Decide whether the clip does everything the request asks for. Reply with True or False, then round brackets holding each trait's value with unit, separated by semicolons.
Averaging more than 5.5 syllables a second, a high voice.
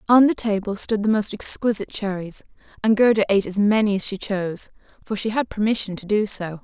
True (6.0 syllables/s; 205 Hz)